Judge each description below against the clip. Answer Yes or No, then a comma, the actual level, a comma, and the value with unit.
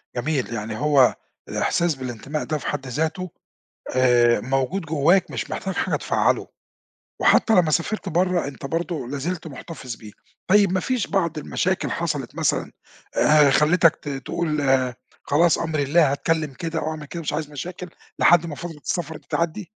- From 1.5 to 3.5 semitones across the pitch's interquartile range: No, average, 3.9 semitones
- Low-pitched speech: No, medium, 155 Hz